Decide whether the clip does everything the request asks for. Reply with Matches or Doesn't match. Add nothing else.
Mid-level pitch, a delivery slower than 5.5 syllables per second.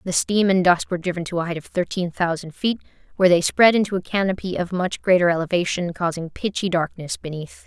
Doesn't match